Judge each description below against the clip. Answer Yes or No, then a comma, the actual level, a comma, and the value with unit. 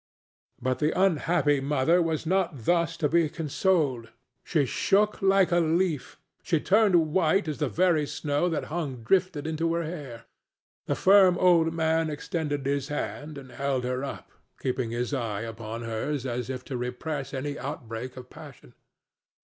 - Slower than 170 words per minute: Yes, average, 160 wpm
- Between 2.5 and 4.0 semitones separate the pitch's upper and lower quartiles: No, average, 4.6 semitones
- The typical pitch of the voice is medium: Yes, medium, 150 Hz